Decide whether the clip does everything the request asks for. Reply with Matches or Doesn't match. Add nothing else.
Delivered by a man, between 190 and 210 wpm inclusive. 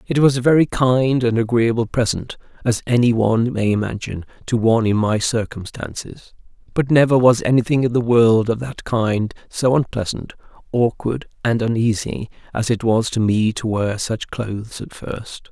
Doesn't match